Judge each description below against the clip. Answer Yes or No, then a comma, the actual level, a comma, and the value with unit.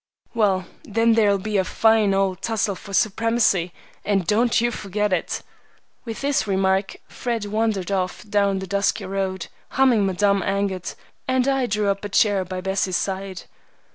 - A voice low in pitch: No, high, 200 Hz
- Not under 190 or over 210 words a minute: No, average, 160 wpm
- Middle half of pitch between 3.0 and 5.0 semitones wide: No, narrow, 2.5 semitones